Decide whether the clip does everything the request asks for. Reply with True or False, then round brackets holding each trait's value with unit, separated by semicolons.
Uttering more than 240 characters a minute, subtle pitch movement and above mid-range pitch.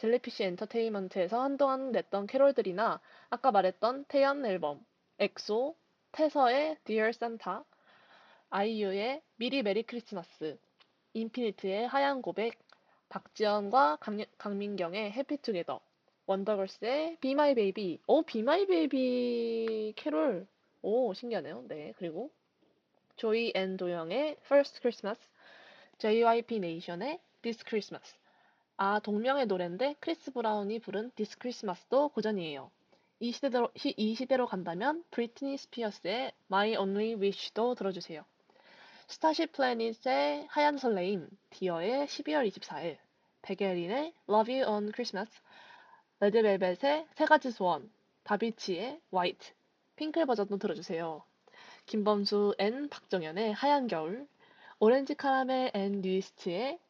False (325 characters per minute; 5.5 semitones; 225 Hz)